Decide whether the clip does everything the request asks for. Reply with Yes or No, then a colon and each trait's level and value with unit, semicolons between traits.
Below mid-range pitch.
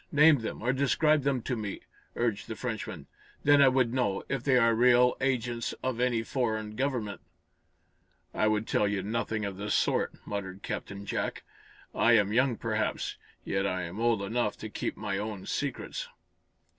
Yes: low, 115 Hz